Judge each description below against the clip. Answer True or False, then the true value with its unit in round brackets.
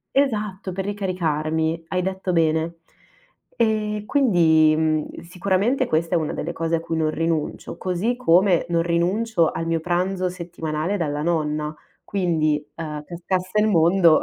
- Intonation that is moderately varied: True (3.1 semitones)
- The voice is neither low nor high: True (170 Hz)